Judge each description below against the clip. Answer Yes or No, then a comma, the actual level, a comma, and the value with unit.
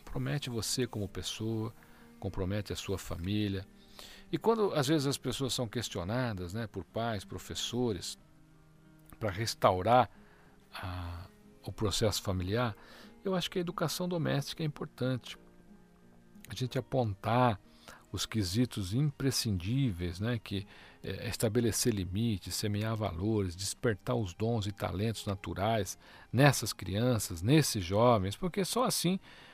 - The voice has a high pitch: No, low, 110 Hz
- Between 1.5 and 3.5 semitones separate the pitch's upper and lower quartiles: No, average, 4.5 semitones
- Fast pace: No, slow, 120 wpm